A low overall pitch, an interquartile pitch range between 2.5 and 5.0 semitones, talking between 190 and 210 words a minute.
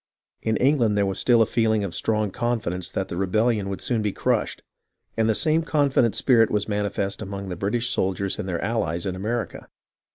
Yes: low, 105 Hz; average, 3.2 semitones; average, 200 wpm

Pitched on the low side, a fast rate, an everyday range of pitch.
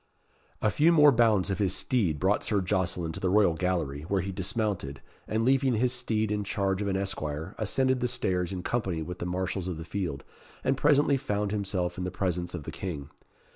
Yes: very low, 95 Hz; fast, 210 wpm; average, 3.7 semitones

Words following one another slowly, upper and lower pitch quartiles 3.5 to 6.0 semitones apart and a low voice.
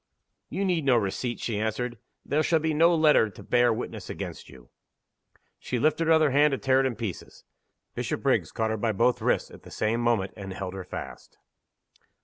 No: average, 195 wpm; wide, 5.6 semitones; low, 120 Hz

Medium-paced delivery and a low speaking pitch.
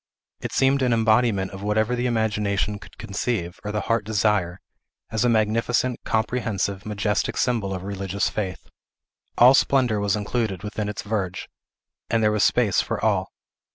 Yes: average, 155 wpm; low, 105 Hz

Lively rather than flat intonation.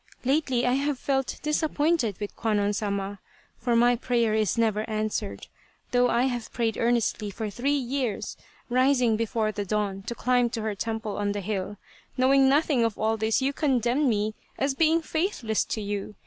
No: average, 3.7 semitones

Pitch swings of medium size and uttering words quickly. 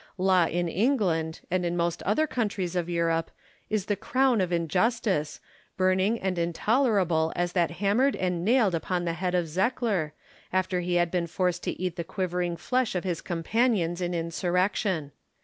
No: average, 3.1 semitones; average, 165 wpm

